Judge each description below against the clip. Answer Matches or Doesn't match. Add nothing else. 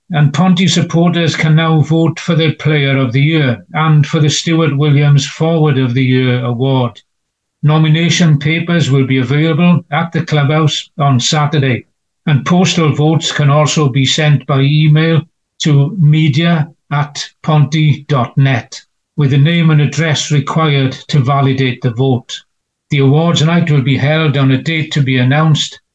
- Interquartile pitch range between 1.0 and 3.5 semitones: Matches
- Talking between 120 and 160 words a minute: Matches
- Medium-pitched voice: Matches